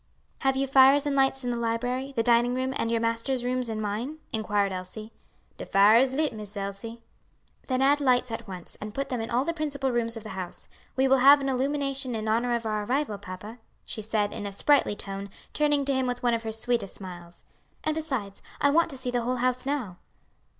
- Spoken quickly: Yes, fast, 225 wpm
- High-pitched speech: Yes, high, 245 Hz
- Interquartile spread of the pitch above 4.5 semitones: No, average, 3.8 semitones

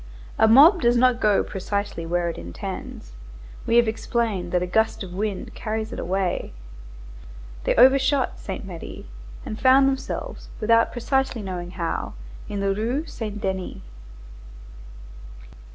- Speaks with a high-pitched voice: Yes, high, 215 Hz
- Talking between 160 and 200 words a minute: No, slow, 135 wpm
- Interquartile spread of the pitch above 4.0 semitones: Yes, average, 4.5 semitones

